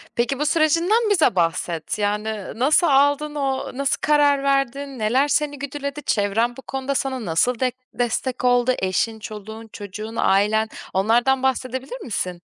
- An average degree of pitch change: Yes, average, 4.5 semitones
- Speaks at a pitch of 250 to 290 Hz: Yes, very high, 255 Hz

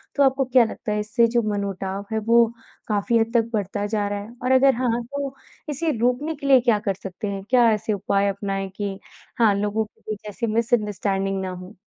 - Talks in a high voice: Yes, high, 215 Hz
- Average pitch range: Yes, average, 3.2 semitones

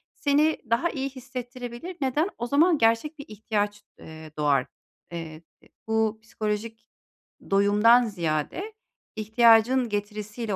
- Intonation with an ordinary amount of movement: Yes, average, 3.8 semitones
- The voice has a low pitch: No, high, 225 Hz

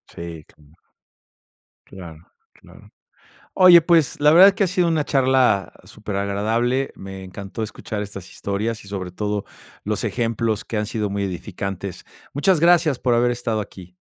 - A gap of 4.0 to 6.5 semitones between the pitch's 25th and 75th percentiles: Yes, average, 5.3 semitones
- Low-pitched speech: Yes, low, 105 Hz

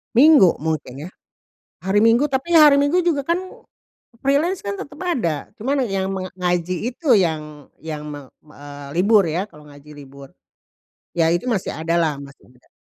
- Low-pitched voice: No, medium, 185 Hz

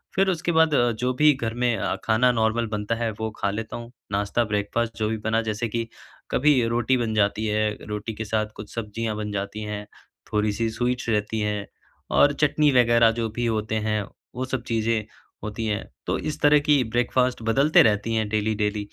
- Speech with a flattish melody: Yes, narrow, 2.3 semitones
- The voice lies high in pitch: No, low, 110 Hz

